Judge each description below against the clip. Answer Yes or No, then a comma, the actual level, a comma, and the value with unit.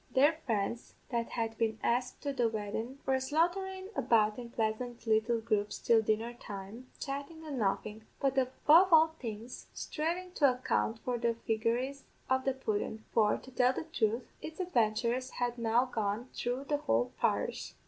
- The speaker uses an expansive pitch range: No, average, 3.7 semitones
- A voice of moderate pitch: No, high, 240 Hz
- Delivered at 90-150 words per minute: No, average, 165 wpm